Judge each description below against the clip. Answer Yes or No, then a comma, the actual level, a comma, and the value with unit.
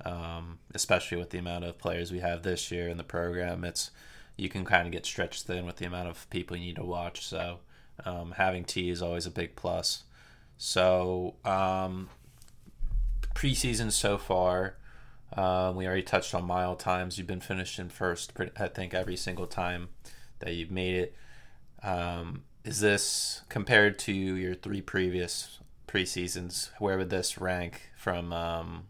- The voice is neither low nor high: No, very low, 90 Hz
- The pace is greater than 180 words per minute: No, average, 170 wpm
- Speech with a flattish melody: Yes, narrow, 1.2 semitones